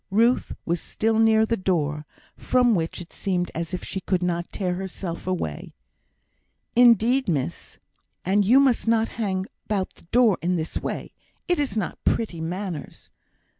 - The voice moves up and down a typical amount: Yes, average, 4.6 semitones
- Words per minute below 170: Yes, average, 160 wpm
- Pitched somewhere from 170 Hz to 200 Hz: Yes, high, 190 Hz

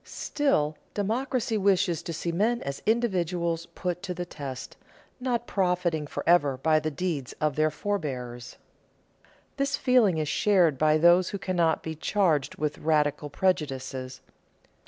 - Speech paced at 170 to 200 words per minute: No, slow, 135 wpm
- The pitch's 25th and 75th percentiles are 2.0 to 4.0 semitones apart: No, average, 4.8 semitones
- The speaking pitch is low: No, medium, 170 Hz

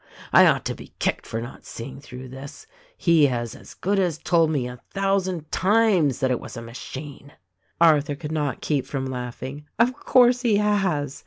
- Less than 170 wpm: No, average, 190 wpm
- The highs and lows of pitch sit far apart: Yes, wide, 6.2 semitones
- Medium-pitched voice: Yes, medium, 150 Hz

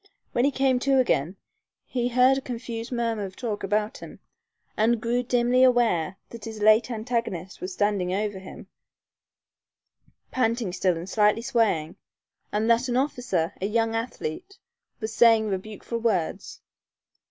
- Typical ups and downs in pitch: Yes, average, 3.2 semitones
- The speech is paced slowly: No, average, 145 wpm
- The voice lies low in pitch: No, high, 225 Hz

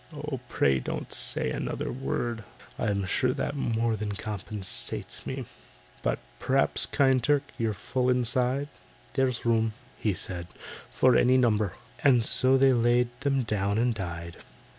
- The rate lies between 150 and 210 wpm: No, average, 140 wpm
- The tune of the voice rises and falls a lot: No, average, 3.7 semitones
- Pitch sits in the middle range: No, low, 120 Hz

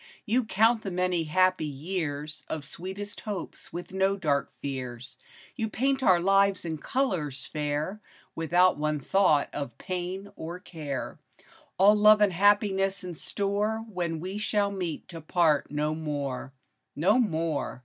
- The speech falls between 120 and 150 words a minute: Yes, average, 145 wpm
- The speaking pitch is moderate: Yes, medium, 180 Hz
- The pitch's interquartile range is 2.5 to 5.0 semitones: Yes, average, 4.7 semitones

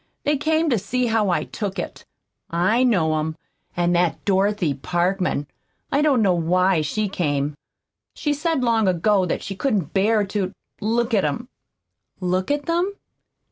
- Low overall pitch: No, high, 195 Hz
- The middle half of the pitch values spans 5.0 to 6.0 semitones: Yes, average, 5.3 semitones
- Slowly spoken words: No, average, 160 wpm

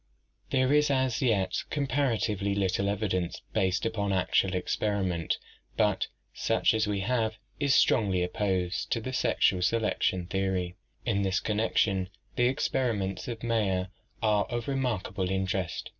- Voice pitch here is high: No, low, 100 Hz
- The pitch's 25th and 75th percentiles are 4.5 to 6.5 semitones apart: No, average, 3.7 semitones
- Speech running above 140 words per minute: No, slow, 135 wpm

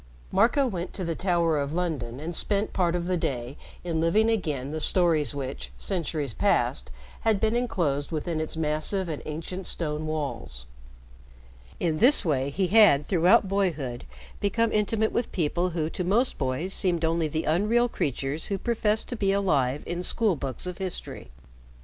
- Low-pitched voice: No, medium, 170 Hz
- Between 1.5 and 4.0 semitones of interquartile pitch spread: No, average, 4.7 semitones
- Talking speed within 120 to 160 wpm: No, average, 170 wpm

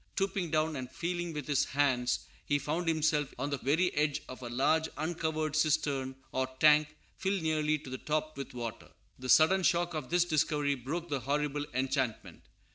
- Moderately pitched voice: Yes, medium, 150 Hz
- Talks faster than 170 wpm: Yes, average, 180 wpm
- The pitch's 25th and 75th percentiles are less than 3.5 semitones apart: Yes, average, 2.8 semitones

